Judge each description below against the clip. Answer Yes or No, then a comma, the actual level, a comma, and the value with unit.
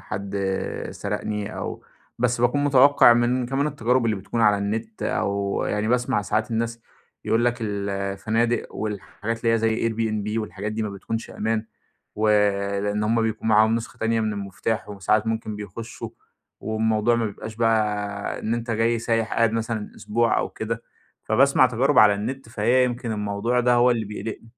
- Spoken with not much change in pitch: Yes, narrow, 2.0 semitones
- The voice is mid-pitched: No, low, 110 Hz